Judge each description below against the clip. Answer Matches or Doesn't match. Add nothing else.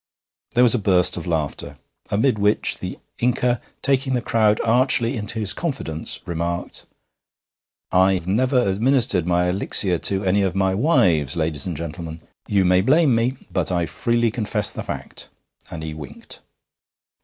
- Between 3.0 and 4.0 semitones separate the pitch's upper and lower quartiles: Doesn't match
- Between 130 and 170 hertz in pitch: Doesn't match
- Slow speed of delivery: Doesn't match